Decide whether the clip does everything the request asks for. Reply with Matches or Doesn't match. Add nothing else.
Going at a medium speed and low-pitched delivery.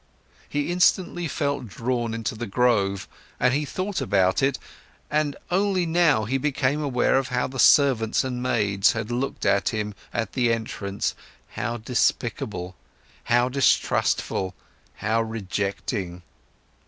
Doesn't match